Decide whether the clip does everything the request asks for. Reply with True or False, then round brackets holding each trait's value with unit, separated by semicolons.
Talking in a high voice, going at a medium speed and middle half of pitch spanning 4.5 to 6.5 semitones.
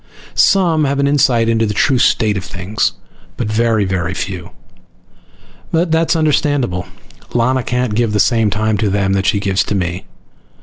False (110 Hz; 175 wpm; 5.4 semitones)